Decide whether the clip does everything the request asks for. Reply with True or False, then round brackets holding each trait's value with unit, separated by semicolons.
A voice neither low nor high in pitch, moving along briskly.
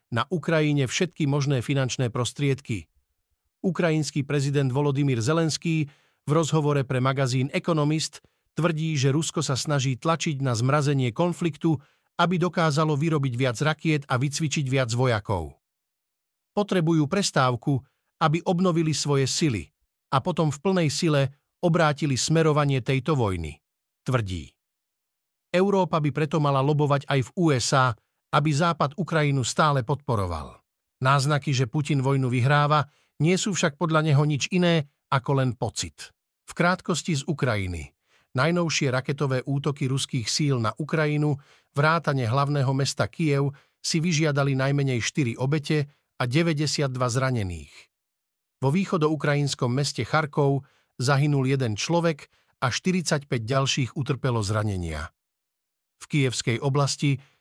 False (145 Hz; 120 wpm)